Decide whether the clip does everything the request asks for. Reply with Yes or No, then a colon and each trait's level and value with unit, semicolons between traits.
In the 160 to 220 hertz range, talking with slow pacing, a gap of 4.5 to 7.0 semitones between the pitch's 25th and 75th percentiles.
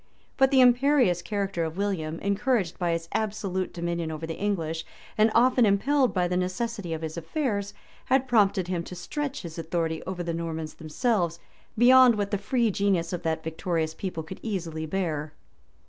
No: medium, 185 Hz; average, 175 wpm; average, 4.9 semitones